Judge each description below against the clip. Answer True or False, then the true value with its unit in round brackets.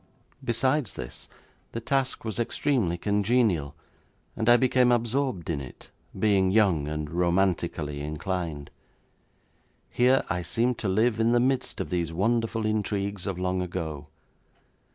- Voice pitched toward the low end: True (100 Hz)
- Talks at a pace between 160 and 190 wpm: False (135 wpm)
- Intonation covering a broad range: True (5.7 semitones)